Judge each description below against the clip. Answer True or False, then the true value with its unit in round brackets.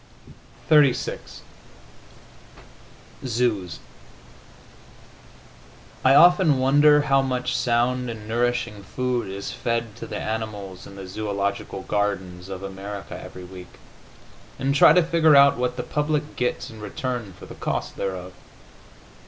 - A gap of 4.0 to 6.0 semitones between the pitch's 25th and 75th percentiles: True (5.2 semitones)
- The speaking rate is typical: False (120 wpm)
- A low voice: True (115 Hz)